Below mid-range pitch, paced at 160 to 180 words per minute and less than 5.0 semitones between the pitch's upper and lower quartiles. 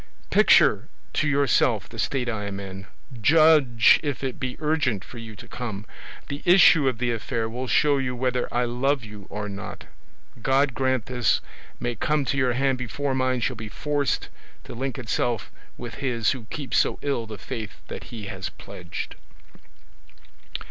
Yes: low, 125 Hz; average, 170 wpm; average, 3.5 semitones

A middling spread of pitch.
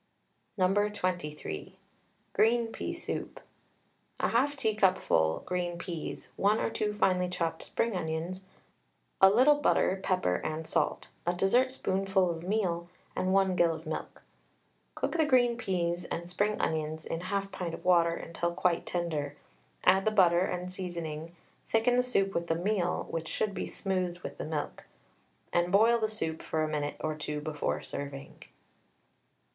Yes: average, 3.5 semitones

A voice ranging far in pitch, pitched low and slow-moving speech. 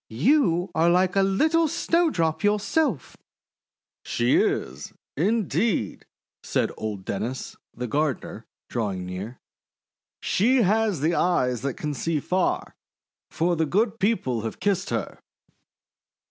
No: wide, 8.8 semitones; medium, 170 Hz; slow, 115 wpm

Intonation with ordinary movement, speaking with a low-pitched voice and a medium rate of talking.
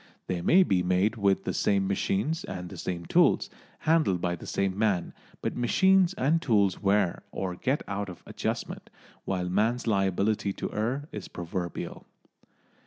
Yes: average, 4.6 semitones; low, 100 Hz; average, 160 wpm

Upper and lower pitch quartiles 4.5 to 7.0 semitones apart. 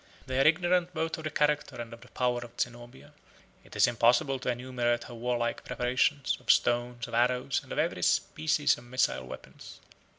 No: average, 3.0 semitones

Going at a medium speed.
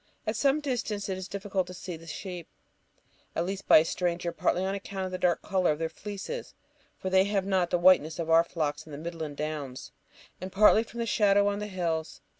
No: fast, 225 wpm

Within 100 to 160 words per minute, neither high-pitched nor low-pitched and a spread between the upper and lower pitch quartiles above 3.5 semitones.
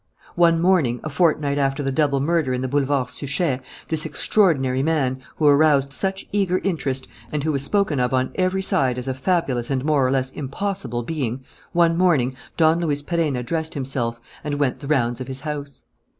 No: average, 190 wpm; medium, 145 Hz; average, 3.9 semitones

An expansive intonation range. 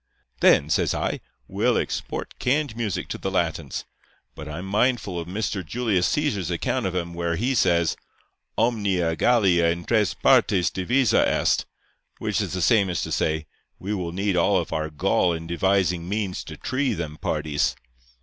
No: average, 4.1 semitones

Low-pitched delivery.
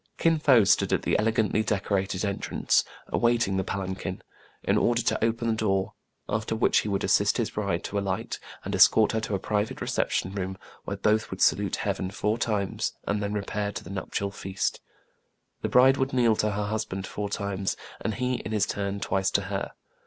Yes: low, 105 Hz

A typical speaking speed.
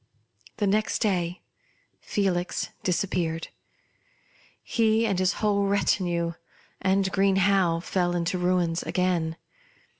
No: slow, 100 wpm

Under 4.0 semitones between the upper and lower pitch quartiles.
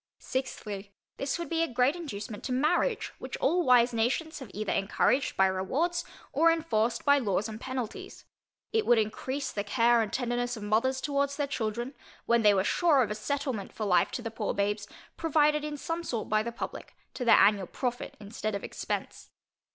No: average, 4.9 semitones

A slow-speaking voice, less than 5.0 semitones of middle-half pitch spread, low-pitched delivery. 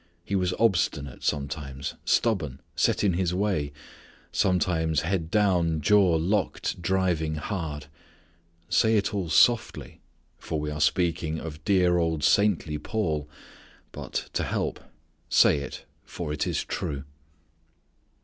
Yes: slow, 125 wpm; average, 4.0 semitones; very low, 85 Hz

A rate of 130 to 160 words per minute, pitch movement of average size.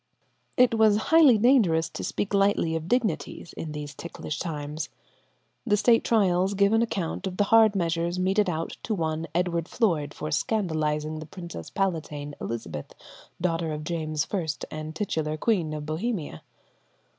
Yes: average, 155 wpm; average, 4.8 semitones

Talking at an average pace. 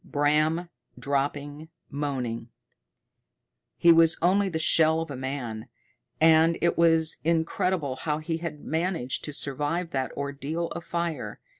No: slow, 130 wpm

